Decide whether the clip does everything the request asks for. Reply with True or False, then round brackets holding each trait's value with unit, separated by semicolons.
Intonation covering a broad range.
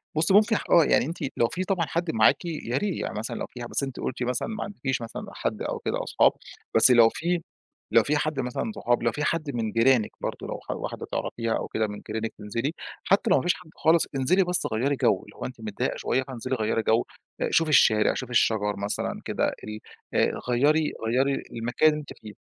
True (5.8 semitones)